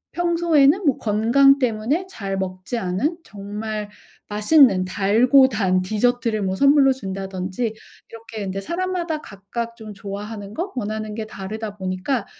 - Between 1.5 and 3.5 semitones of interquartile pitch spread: No, wide, 5.5 semitones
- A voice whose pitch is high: Yes, high, 220 Hz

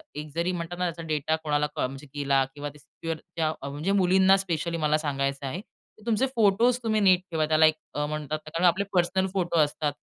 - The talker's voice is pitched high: No, medium, 160 Hz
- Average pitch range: Yes, average, 3.8 semitones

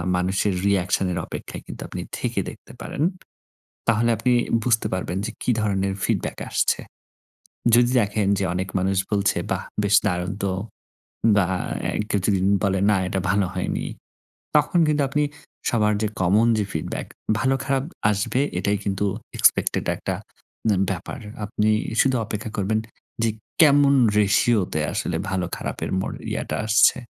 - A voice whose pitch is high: No, low, 105 Hz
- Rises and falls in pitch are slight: No, average, 3.3 semitones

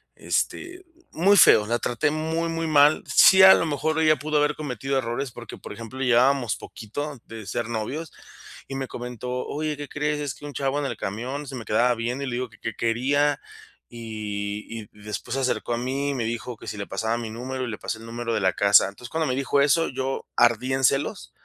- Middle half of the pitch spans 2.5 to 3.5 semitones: No, average, 4.1 semitones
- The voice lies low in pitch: Yes, low, 130 Hz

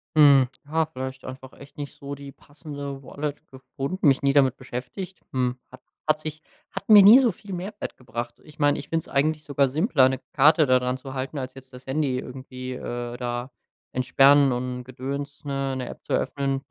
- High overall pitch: No, low, 135 Hz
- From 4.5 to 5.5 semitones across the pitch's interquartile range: No, narrow, 2.5 semitones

